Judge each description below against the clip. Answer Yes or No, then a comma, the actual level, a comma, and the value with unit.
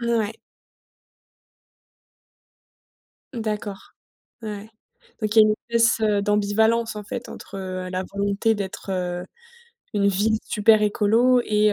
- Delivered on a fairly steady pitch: Yes, narrow, 1.8 semitones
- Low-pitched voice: No, high, 210 Hz